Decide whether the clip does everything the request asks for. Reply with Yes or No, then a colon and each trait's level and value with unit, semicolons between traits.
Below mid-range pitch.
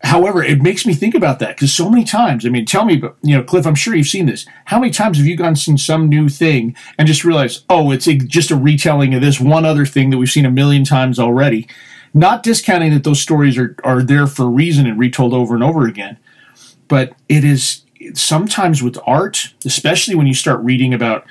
No: medium, 145 Hz